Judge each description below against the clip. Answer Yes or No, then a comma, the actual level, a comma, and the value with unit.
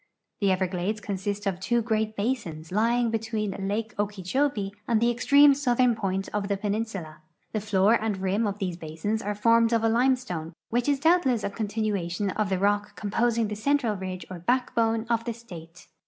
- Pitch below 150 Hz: No, high, 215 Hz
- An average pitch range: Yes, average, 3.2 semitones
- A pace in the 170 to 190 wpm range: Yes, average, 180 wpm